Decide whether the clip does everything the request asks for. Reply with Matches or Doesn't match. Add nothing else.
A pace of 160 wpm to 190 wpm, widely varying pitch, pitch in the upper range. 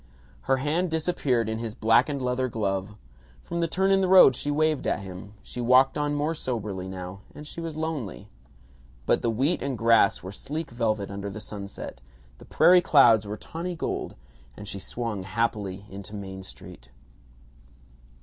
Doesn't match